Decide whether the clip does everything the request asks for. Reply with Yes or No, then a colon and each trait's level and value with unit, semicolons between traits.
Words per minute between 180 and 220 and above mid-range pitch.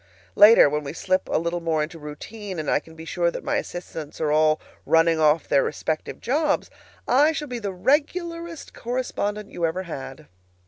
No: average, 185 wpm; medium, 170 Hz